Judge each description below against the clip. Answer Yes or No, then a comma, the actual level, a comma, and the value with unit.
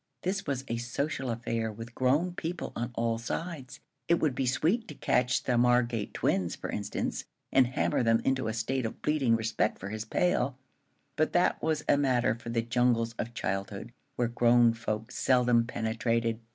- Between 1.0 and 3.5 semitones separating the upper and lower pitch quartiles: Yes, average, 2.8 semitones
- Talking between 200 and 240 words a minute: No, average, 180 wpm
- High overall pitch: No, low, 120 Hz